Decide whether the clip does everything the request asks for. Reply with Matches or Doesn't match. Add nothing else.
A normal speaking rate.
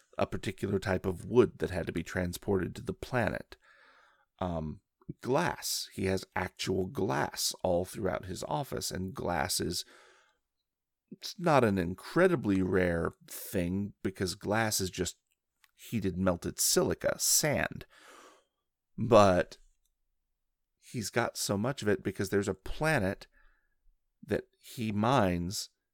Doesn't match